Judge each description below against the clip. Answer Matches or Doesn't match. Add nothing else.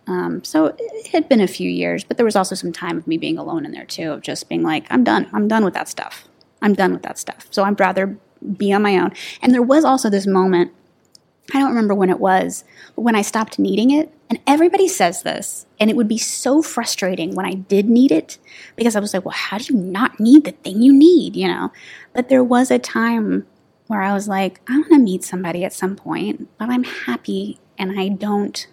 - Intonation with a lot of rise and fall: Matches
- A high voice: Matches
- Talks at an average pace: Doesn't match